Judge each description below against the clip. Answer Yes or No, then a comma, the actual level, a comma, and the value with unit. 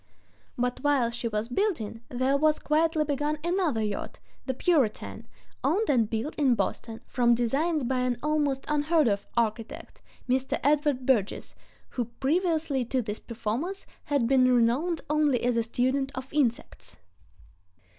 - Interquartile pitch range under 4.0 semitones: No, average, 4.3 semitones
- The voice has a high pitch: Yes, very high, 265 Hz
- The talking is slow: No, average, 145 wpm